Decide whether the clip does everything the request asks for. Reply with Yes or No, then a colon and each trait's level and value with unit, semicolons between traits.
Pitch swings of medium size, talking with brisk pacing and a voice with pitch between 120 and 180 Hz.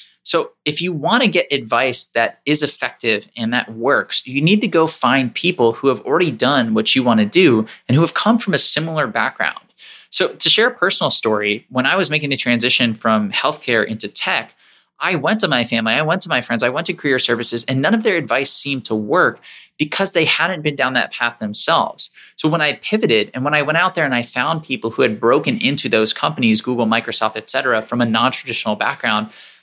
No: wide, 5.9 semitones; fast, 225 wpm; low, 135 Hz